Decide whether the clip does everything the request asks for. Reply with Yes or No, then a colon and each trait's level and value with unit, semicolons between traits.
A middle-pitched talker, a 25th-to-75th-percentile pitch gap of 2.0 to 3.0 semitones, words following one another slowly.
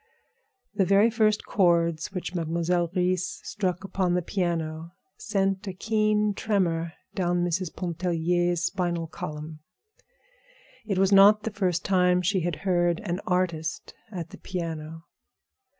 Yes: medium, 180 Hz; narrow, 2.4 semitones; slow, 130 wpm